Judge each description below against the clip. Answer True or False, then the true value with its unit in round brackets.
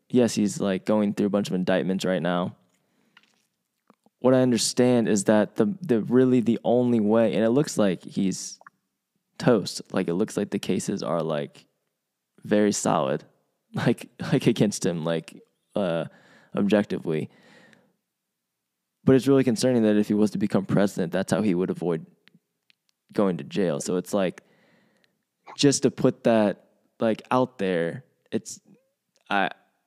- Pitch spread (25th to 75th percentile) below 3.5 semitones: False (4.2 semitones)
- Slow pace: False (155 wpm)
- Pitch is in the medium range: False (110 Hz)